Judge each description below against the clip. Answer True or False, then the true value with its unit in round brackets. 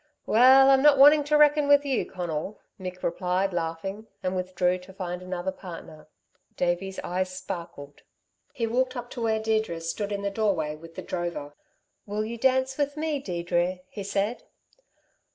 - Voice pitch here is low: False (195 Hz)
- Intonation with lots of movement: True (5.9 semitones)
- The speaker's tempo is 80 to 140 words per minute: False (165 wpm)